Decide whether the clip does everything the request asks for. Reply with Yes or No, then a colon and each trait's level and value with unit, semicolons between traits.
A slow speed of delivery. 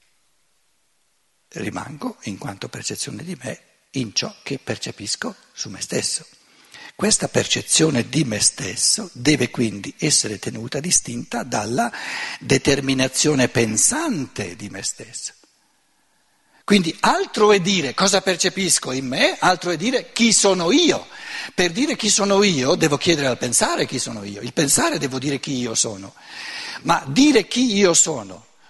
No: average, 140 wpm